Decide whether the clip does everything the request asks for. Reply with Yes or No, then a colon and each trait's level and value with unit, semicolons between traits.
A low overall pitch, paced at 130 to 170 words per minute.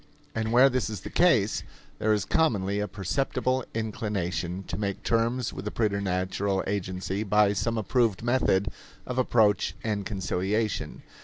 Yes: low, 105 Hz; average, 145 wpm